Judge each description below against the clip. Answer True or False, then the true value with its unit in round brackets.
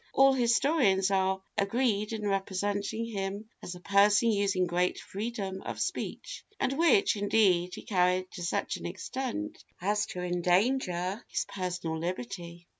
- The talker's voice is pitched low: False (200 Hz)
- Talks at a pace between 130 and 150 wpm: True (140 wpm)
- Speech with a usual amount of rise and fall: True (3.6 semitones)